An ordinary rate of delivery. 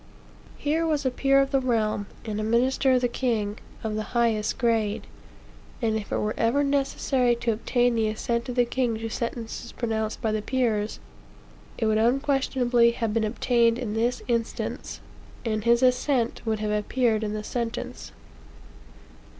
Yes: average, 165 wpm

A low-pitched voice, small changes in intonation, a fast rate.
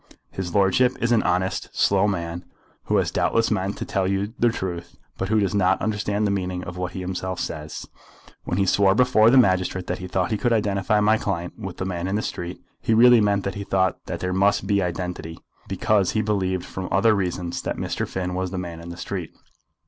Yes: very low, 95 Hz; narrow, 2.3 semitones; fast, 225 wpm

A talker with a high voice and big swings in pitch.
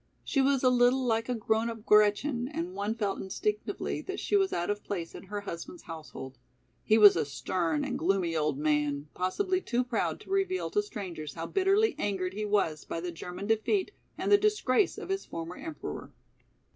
Yes: high, 210 Hz; wide, 8.2 semitones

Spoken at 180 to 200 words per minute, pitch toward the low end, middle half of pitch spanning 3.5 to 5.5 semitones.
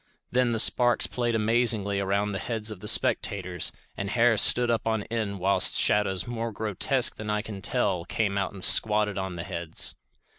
No: average, 185 wpm; low, 105 Hz; average, 2.7 semitones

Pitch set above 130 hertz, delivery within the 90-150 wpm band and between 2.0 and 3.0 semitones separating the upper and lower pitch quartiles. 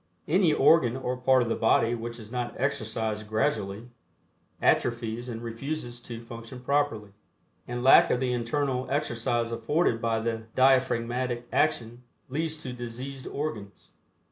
No: low, 120 Hz; average, 140 wpm; narrow, 2.4 semitones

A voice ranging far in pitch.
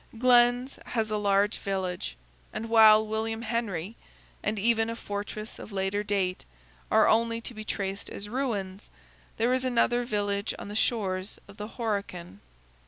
No: narrow, 2.5 semitones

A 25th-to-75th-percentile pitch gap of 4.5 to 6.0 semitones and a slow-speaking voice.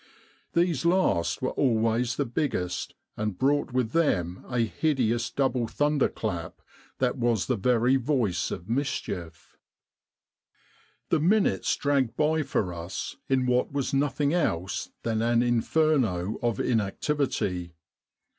Yes: average, 4.9 semitones; slow, 125 wpm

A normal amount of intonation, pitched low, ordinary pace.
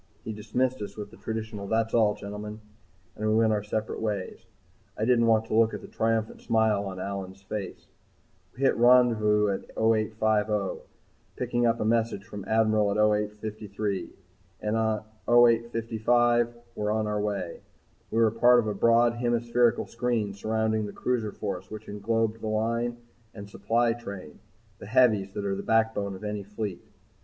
No: narrow, 1.8 semitones; low, 110 Hz; average, 165 wpm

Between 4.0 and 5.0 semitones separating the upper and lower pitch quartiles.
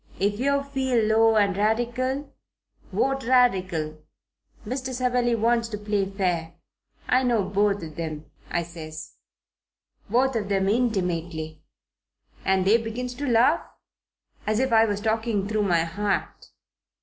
Yes: average, 4.4 semitones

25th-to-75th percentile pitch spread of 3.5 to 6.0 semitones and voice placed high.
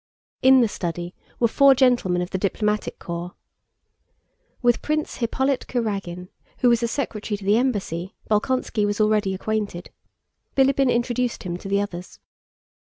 Yes: average, 4.6 semitones; high, 215 Hz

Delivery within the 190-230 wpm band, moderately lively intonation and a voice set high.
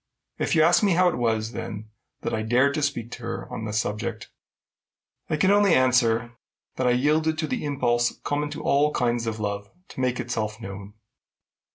No: average, 195 wpm; average, 4.8 semitones; low, 120 Hz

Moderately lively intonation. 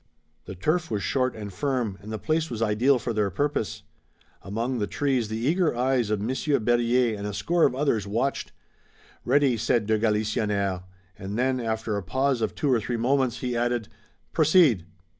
Yes: average, 3.9 semitones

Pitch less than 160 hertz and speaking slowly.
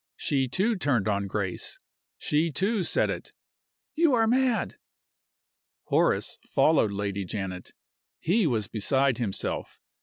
Yes: low, 135 Hz; slow, 120 wpm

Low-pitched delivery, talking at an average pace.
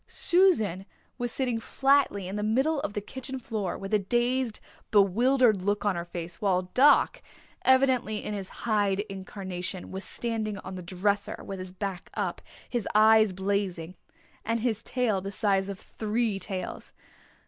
No: high, 205 Hz; average, 160 wpm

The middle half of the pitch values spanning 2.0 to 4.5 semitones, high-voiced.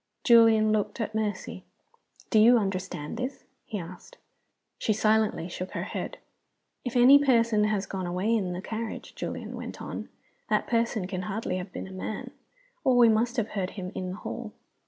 Yes: average, 3.6 semitones; high, 215 Hz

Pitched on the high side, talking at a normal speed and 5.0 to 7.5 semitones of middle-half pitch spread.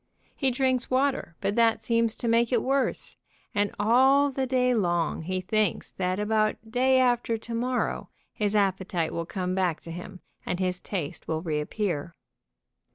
Yes: high, 215 Hz; average, 160 wpm; wide, 5.4 semitones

